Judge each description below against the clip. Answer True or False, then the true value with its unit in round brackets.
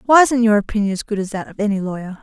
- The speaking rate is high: True (295 wpm)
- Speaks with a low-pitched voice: False (210 Hz)